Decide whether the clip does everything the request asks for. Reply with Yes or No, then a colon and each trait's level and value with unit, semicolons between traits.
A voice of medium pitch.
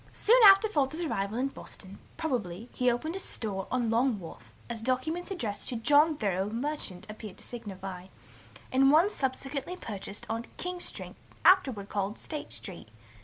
No: high, 245 Hz